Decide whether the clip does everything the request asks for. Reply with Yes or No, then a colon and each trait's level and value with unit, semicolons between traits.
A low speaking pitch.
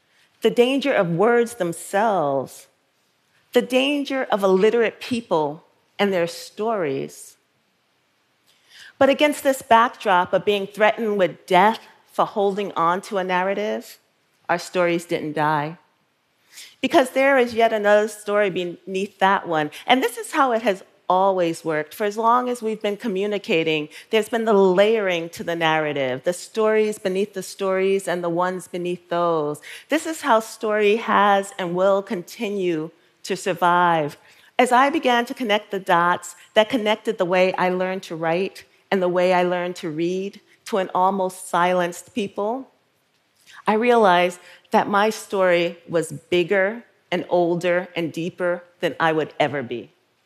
No: high, 190 Hz